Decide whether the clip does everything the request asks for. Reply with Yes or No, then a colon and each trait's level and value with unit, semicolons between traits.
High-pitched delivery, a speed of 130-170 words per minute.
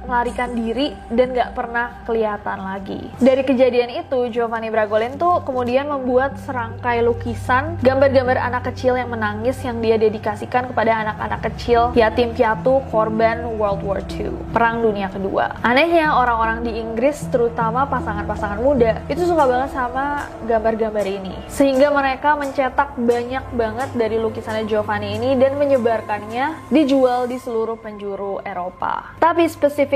Yes: high, 240 Hz; average, 135 wpm